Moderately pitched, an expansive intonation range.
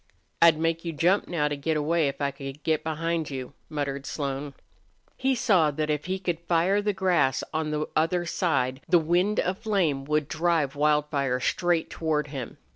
No: medium, 155 Hz; average, 3.2 semitones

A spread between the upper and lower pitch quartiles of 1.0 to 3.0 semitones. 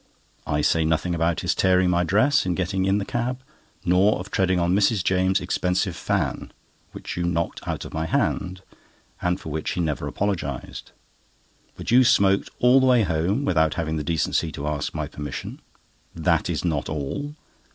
No: average, 3.6 semitones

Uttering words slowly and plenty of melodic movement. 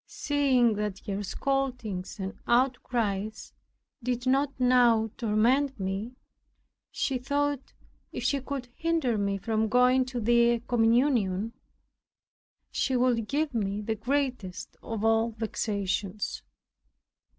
No: slow, 110 wpm; average, 3.4 semitones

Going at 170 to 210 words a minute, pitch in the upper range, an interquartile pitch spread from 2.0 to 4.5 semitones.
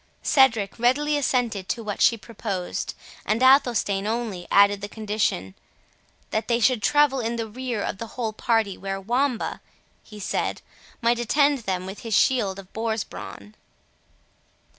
No: average, 150 wpm; high, 225 Hz; average, 3.5 semitones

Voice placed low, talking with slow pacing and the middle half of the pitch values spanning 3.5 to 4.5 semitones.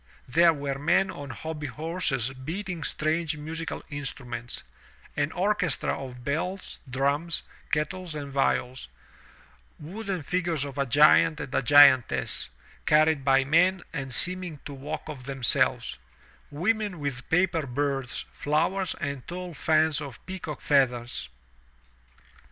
No: medium, 150 Hz; slow, 120 wpm; average, 3.8 semitones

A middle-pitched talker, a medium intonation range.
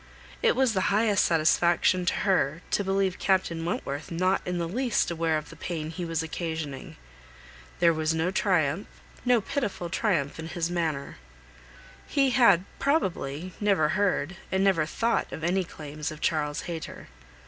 Yes: medium, 175 Hz; average, 3.4 semitones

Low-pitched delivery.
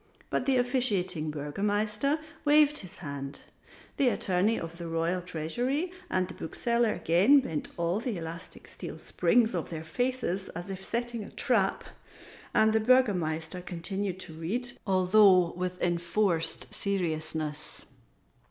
No: medium, 185 Hz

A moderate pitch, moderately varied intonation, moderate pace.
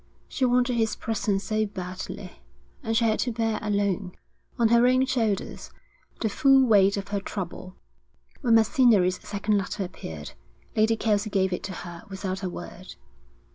No: high, 210 Hz; average, 3.1 semitones; average, 160 wpm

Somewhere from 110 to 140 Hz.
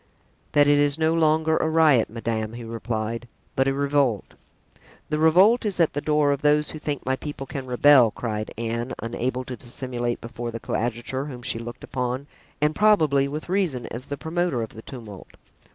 Yes: low, 135 Hz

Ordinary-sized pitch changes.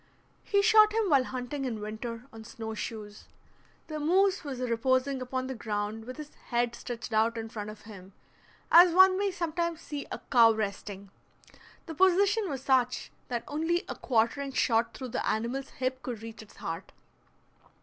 No: wide, 5.7 semitones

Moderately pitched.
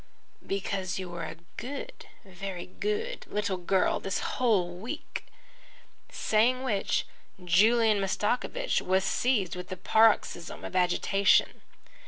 No: high, 195 Hz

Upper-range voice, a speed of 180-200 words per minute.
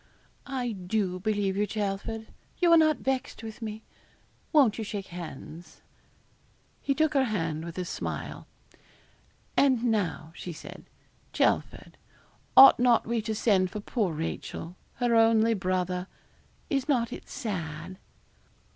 No: high, 215 Hz; slow, 135 wpm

